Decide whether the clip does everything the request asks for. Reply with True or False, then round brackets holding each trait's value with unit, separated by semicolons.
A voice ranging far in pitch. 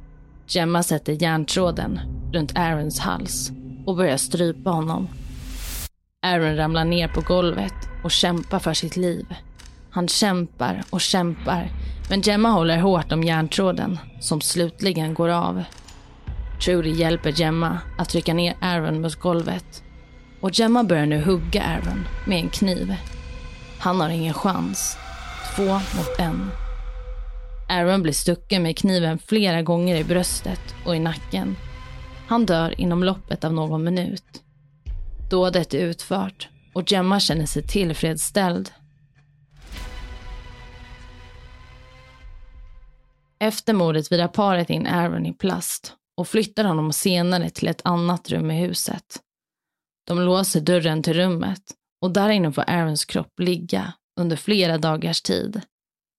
False (3.6 semitones)